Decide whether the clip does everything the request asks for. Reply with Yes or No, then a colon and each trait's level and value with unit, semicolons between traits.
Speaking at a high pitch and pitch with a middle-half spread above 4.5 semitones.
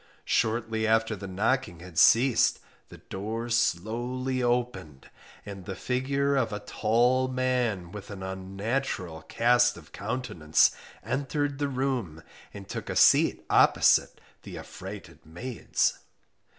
No: low, 115 Hz; average, 5.1 semitones